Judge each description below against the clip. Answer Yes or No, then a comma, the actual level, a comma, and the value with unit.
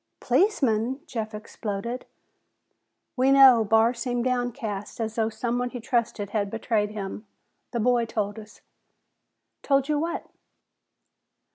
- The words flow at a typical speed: No, slow, 120 wpm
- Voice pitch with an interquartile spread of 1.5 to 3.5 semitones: Yes, average, 2.7 semitones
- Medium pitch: No, high, 235 Hz